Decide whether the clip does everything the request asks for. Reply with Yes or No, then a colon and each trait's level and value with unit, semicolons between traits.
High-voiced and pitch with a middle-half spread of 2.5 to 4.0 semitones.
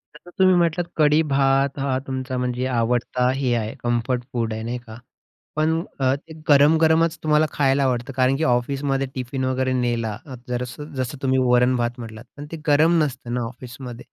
No: low, 130 Hz; average, 2.9 semitones